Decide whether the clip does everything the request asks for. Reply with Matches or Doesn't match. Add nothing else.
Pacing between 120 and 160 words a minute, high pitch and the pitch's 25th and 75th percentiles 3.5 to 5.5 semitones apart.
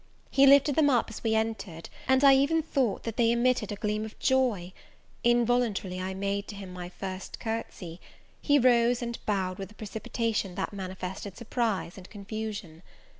Doesn't match